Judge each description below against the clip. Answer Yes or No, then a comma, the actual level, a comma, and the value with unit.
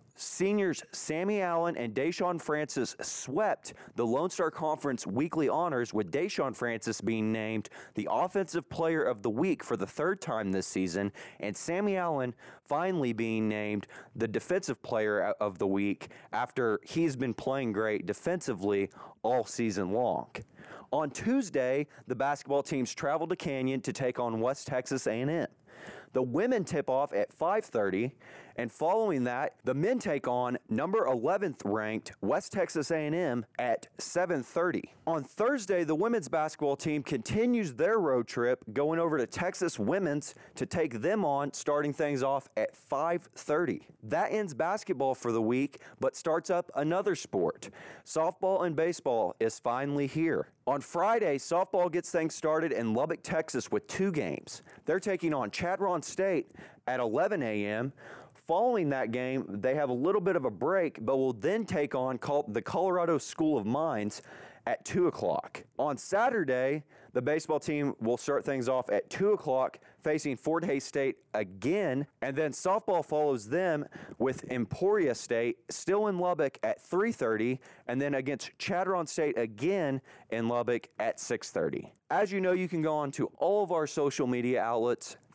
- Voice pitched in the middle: Yes, medium, 145 Hz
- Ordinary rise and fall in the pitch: No, wide, 5.7 semitones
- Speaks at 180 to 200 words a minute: No, average, 160 wpm